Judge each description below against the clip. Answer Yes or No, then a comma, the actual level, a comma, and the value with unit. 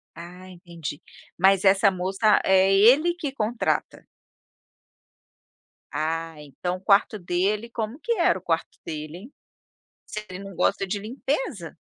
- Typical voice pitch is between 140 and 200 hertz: Yes, high, 195 Hz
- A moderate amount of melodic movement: Yes, average, 3.5 semitones